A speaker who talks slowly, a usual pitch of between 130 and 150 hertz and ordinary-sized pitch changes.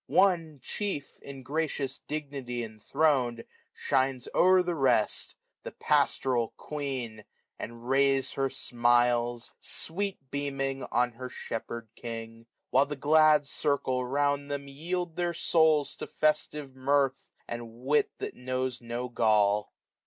Yes: slow, 125 wpm; low, 135 Hz; average, 3.6 semitones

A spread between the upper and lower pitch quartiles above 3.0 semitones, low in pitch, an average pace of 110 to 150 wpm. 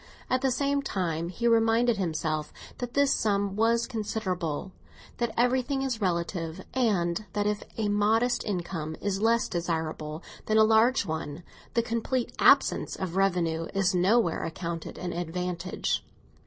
No: average, 5.2 semitones; high, 200 Hz; average, 140 wpm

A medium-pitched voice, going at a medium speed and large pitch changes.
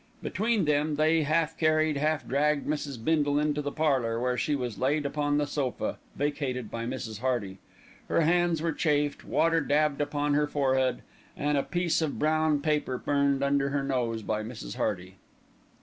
No: medium, 145 Hz; average, 170 wpm; average, 2.7 semitones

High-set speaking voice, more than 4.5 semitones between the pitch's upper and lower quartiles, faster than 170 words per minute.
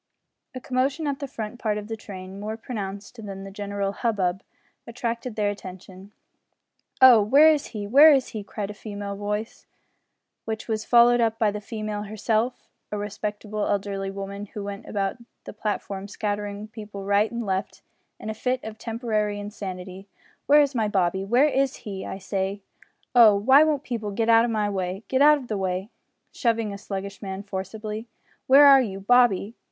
No: high, 210 Hz; average, 2.7 semitones; average, 180 wpm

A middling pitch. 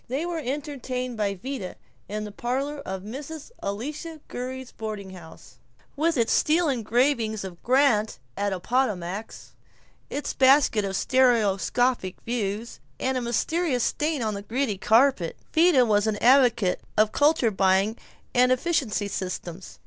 No: high, 240 Hz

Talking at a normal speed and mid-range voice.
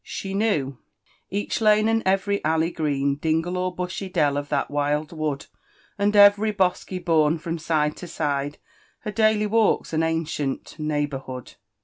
Yes: average, 155 wpm; medium, 165 Hz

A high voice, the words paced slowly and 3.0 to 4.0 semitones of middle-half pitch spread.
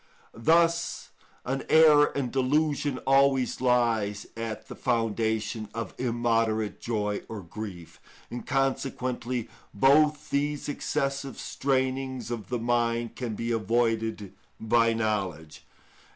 No: low, 120 Hz; slow, 110 wpm; average, 3.5 semitones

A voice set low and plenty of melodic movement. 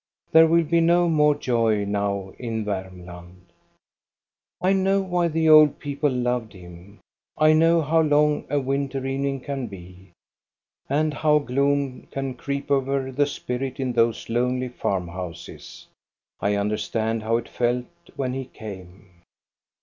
Yes: low, 130 Hz; wide, 5.9 semitones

